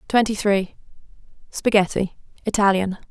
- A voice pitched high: Yes, high, 200 Hz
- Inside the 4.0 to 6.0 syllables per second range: Yes, 5.1 syllables/s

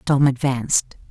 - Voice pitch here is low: Yes, low, 130 Hz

